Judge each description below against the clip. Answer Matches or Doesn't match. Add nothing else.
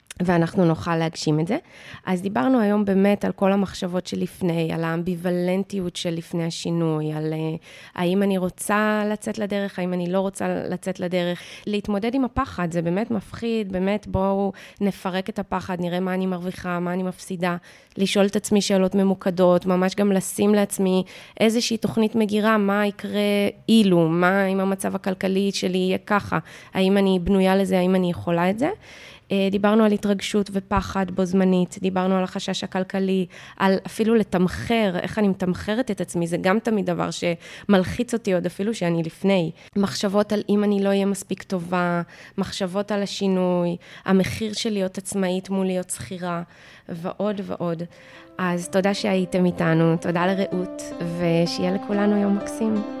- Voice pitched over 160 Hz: Matches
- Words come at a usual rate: Matches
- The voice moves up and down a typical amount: Doesn't match